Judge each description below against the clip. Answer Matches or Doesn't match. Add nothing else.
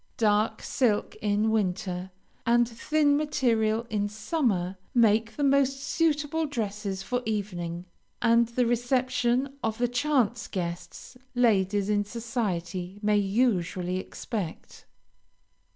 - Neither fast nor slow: Doesn't match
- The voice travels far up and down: Doesn't match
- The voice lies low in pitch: Doesn't match